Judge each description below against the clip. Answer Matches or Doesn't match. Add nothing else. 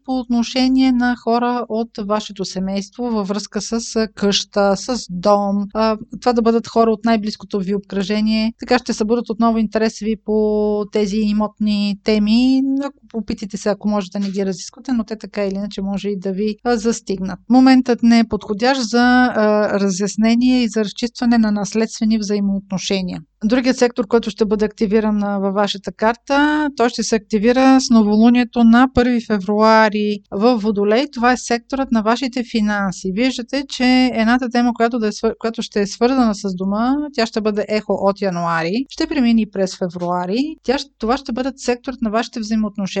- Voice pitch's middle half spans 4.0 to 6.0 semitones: Doesn't match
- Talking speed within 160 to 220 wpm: Matches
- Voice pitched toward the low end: Doesn't match